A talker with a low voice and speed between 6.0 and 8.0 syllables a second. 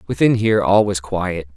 No: very low, 95 Hz; 5.2 syllables/s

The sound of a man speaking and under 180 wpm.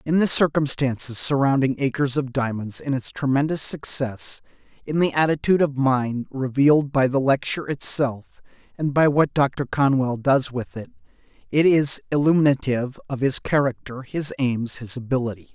Yes: male; average, 150 wpm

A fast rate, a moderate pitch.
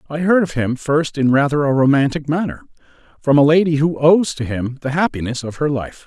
Yes: fast, 220 wpm; medium, 145 Hz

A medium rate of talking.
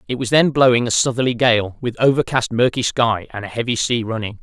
No: fast, 215 wpm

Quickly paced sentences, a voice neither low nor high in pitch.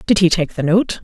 Yes: fast, 290 wpm; medium, 170 Hz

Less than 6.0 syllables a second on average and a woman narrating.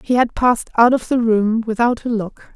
Yes: 5.1 syllables/s; female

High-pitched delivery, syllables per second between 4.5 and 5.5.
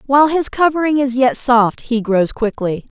Yes: very high, 255 Hz; 4.7 syllables/s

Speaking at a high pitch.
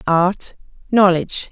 No: medium, 180 Hz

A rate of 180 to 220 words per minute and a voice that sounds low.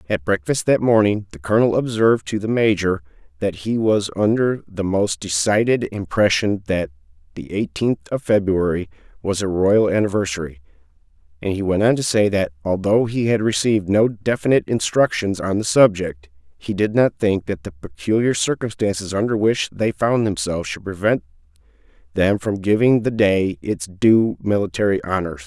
No: average, 160 wpm; low, 100 Hz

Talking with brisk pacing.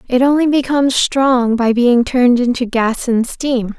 No: average, 175 wpm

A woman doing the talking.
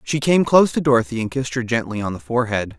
No: male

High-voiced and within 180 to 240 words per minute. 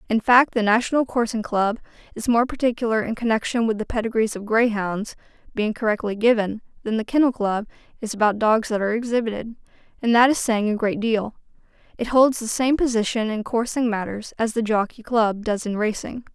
Yes: high, 225 Hz; average, 185 wpm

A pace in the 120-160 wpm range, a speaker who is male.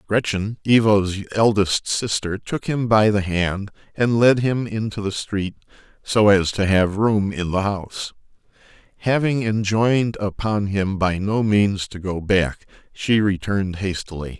Yes: average, 150 wpm; male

